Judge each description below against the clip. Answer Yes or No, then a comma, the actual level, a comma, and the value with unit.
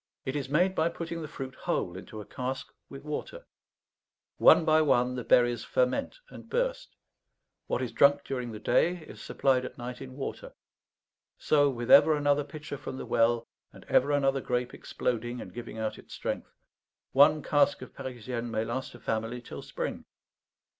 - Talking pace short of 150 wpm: No, average, 175 wpm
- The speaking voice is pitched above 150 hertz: No, low, 130 Hz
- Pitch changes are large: No, average, 3.4 semitones